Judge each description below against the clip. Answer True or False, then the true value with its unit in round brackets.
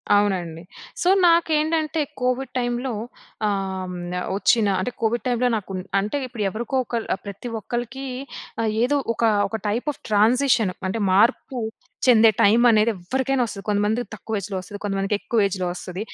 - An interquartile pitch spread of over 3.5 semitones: True (4.0 semitones)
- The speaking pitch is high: True (220 Hz)